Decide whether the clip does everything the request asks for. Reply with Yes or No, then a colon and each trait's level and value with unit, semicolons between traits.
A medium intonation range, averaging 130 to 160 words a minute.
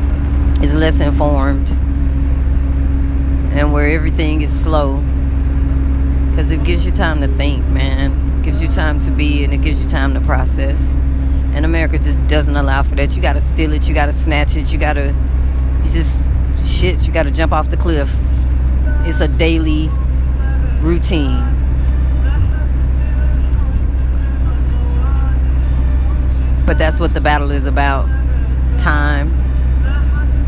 No: narrow, 1.2 semitones; average, 140 wpm